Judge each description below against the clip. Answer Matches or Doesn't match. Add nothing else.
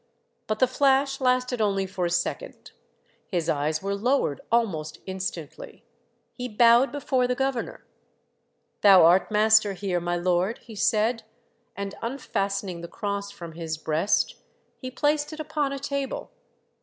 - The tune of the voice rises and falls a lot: Matches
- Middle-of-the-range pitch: Doesn't match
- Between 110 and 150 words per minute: Matches